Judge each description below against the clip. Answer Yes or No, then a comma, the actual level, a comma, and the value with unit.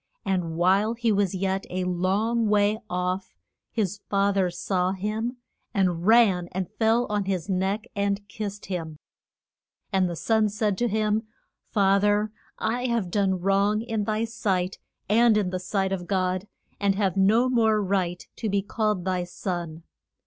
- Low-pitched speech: No, high, 200 Hz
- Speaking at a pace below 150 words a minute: No, average, 165 wpm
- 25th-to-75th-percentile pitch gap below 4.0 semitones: Yes, average, 2.7 semitones